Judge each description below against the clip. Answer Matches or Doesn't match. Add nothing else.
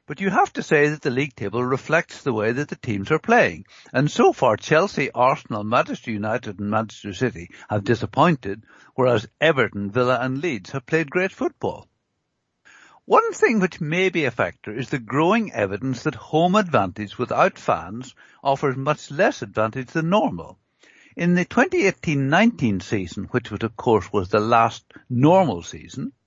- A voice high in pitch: Doesn't match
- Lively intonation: Matches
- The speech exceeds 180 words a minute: Doesn't match